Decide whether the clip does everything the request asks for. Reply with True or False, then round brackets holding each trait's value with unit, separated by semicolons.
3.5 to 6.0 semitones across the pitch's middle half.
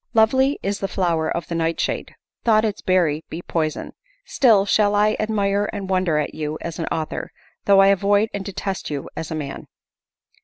True (4.0 semitones)